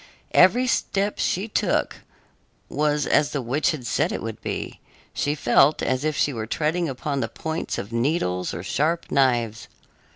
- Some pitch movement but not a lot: Yes, average, 5.0 semitones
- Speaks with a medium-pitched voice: Yes, medium, 145 Hz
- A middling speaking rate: Yes, average, 170 wpm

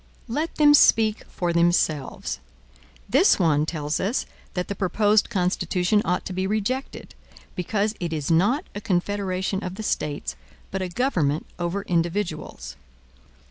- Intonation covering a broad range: No, average, 3.7 semitones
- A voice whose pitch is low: No, medium, 185 Hz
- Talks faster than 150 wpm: No, average, 140 wpm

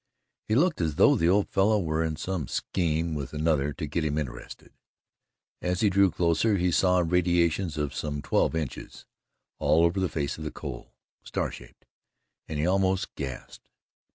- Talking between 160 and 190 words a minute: Yes, average, 175 wpm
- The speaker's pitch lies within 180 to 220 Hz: No, very low, 85 Hz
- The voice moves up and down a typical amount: Yes, average, 3.4 semitones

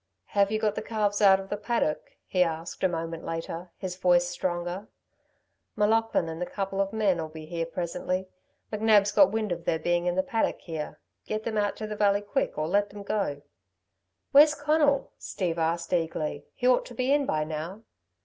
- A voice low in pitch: No, high, 190 Hz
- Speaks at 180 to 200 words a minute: Yes, average, 195 wpm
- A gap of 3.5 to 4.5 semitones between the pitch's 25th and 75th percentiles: Yes, average, 4.2 semitones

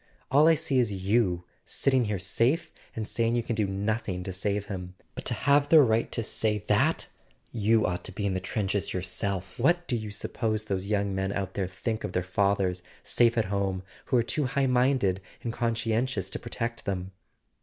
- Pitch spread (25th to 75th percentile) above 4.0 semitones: No, average, 3.7 semitones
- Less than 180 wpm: No, average, 200 wpm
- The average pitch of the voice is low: Yes, low, 105 Hz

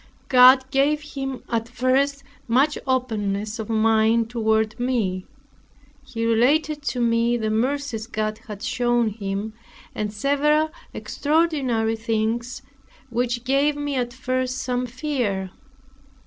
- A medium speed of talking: No, slow, 120 wpm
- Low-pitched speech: No, high, 240 Hz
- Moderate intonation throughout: Yes, average, 3.4 semitones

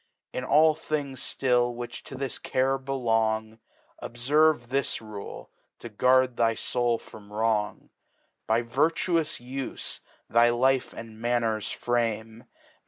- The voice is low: Yes, low, 120 Hz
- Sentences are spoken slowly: Yes, slow, 120 wpm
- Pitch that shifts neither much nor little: Yes, average, 3.0 semitones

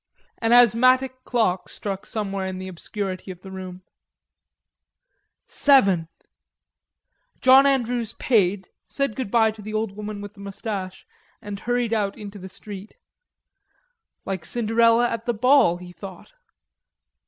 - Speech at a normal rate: No, slow, 130 wpm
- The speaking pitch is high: Yes, high, 210 Hz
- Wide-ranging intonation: No, average, 3.8 semitones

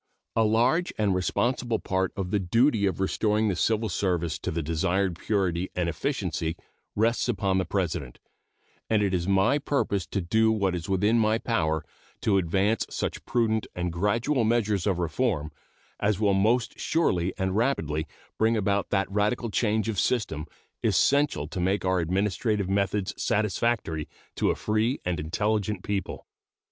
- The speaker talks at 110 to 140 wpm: No, average, 155 wpm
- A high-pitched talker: No, low, 100 Hz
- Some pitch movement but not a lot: Yes, average, 3.5 semitones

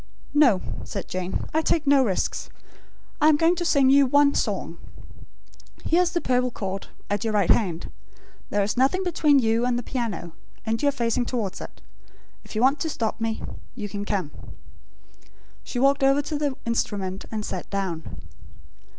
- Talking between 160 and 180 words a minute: Yes, average, 175 wpm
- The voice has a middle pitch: No, high, 245 Hz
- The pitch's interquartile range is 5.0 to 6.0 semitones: Yes, wide, 5.6 semitones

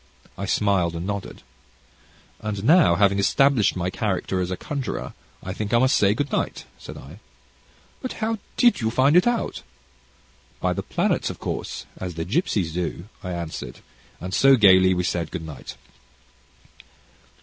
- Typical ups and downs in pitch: No, wide, 6.5 semitones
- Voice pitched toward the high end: No, low, 100 Hz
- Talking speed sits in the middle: Yes, average, 160 wpm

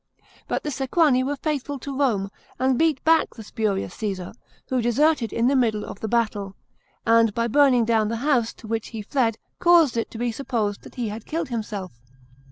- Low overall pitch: No, high, 235 Hz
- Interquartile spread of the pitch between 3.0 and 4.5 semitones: Yes, average, 4.0 semitones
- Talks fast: No, average, 195 wpm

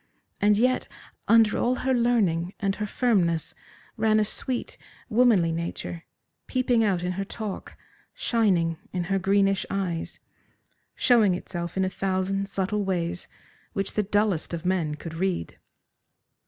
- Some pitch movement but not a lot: Yes, average, 3.7 semitones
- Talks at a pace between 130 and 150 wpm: Yes, average, 140 wpm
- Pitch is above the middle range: Yes, high, 195 Hz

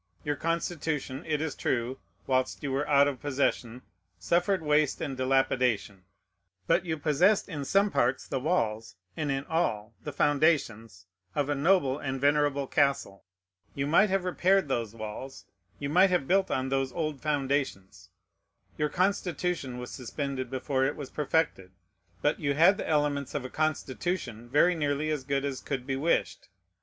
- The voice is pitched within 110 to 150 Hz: Yes, medium, 140 Hz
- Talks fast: No, average, 160 wpm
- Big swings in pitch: No, average, 3.3 semitones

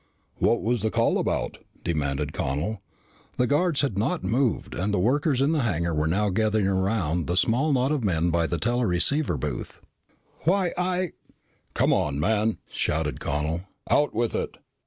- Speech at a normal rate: Yes, average, 170 wpm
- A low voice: Yes, low, 105 Hz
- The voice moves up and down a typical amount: No, wide, 7.9 semitones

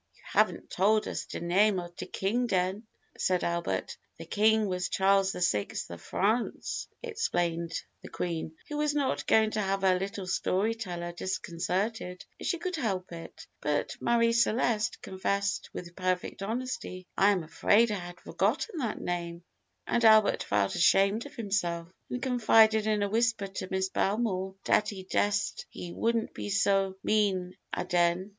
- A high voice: Yes, high, 195 Hz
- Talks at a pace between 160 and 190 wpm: Yes, average, 165 wpm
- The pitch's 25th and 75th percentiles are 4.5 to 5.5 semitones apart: No, average, 3.5 semitones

